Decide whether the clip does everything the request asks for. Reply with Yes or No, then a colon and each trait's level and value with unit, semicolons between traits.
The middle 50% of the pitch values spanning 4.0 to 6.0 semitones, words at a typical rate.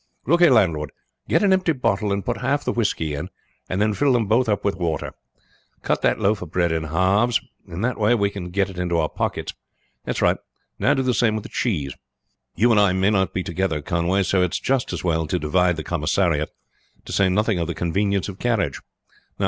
No: average, 4.3 semitones; fast, 220 wpm